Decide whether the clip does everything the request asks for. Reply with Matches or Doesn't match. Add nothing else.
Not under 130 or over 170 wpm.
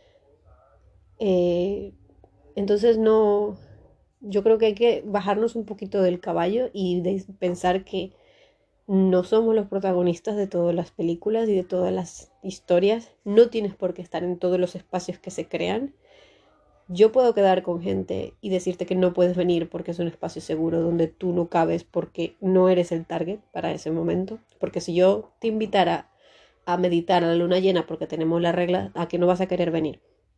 Doesn't match